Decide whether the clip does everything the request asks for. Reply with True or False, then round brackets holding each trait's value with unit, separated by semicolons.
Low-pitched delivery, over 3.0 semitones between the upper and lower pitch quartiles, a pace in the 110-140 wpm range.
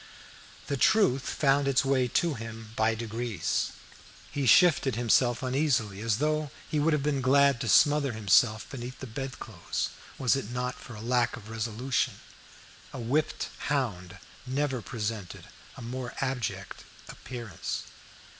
True (125 Hz; 3.5 semitones; 135 wpm)